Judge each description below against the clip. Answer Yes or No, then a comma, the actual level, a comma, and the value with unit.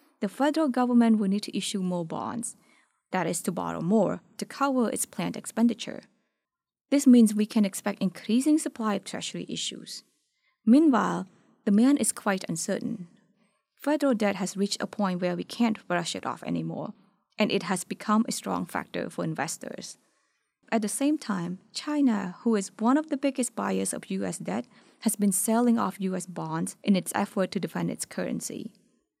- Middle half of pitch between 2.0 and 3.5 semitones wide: No, average, 4.1 semitones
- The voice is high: Yes, high, 215 Hz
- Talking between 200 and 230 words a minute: No, average, 175 wpm